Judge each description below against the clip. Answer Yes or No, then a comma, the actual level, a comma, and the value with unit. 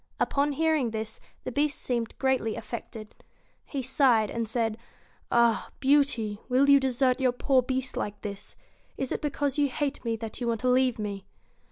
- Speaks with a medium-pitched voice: No, very high, 250 Hz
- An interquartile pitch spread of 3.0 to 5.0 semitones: Yes, average, 3.5 semitones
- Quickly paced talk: No, average, 175 wpm